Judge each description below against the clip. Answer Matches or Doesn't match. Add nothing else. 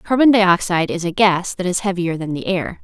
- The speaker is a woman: Matches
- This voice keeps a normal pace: Doesn't match